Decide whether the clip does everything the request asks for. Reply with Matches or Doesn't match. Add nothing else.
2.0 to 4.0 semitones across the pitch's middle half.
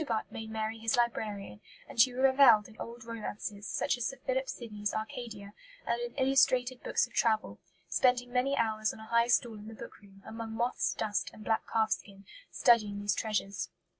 Matches